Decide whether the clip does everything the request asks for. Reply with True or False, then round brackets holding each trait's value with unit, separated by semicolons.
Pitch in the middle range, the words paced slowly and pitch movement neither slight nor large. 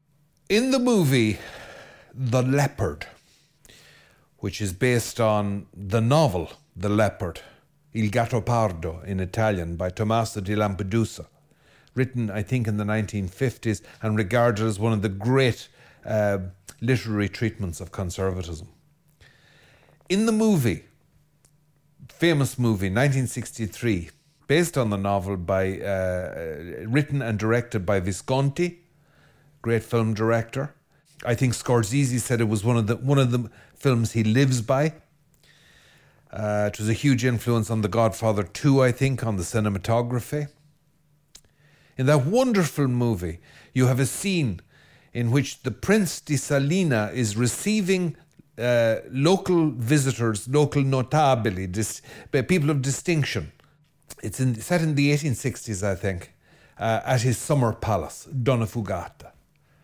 False (120 Hz; 130 wpm; 5.0 semitones)